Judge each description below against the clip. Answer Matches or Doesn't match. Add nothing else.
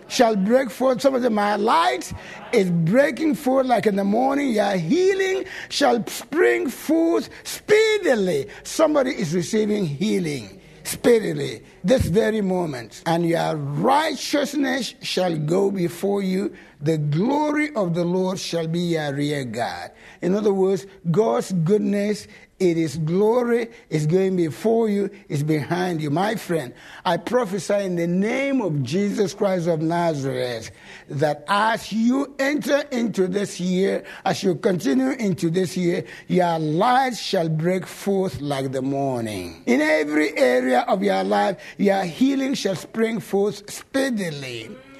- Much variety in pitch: Matches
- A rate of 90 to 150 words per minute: Matches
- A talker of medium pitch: Doesn't match